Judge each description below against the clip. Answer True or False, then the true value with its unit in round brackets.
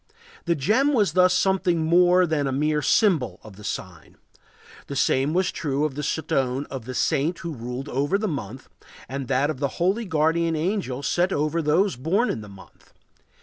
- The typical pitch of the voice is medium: True (150 Hz)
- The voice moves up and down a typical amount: True (5.0 semitones)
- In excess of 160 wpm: True (185 wpm)